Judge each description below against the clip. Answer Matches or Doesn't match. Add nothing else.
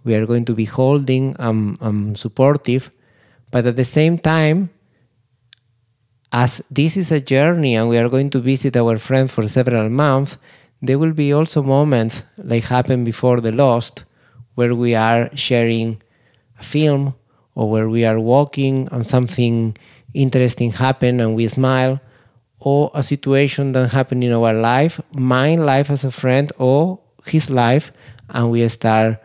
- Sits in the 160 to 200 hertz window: Doesn't match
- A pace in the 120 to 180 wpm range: Matches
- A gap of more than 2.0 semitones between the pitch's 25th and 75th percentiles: Matches